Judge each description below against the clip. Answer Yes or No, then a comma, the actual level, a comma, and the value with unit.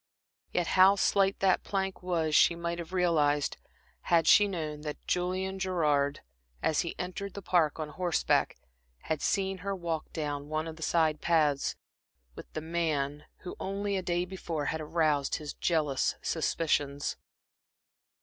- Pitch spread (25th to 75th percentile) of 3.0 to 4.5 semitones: Yes, average, 3.4 semitones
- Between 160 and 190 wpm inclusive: No, average, 150 wpm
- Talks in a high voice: No, medium, 165 Hz